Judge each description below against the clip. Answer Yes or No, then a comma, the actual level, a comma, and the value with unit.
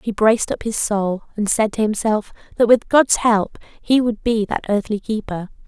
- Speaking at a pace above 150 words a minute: Yes, average, 200 wpm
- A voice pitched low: No, high, 215 Hz